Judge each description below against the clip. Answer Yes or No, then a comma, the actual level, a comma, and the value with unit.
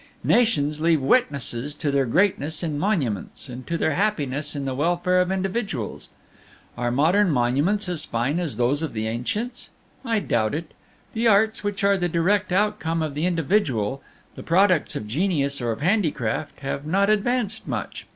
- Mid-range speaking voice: Yes, medium, 160 Hz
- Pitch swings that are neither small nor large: No, wide, 6.4 semitones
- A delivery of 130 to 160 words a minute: No, average, 170 wpm